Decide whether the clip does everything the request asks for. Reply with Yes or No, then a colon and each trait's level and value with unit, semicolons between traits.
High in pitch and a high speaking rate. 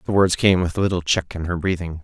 No: very low, 90 Hz; fast, 295 wpm